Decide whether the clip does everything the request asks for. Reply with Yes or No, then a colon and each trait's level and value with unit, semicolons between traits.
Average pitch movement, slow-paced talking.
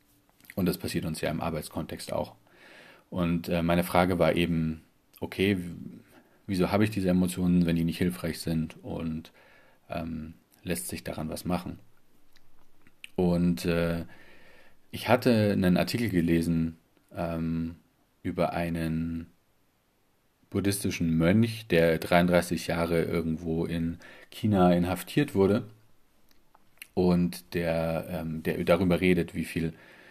No: narrow, 1.6 semitones; slow, 120 wpm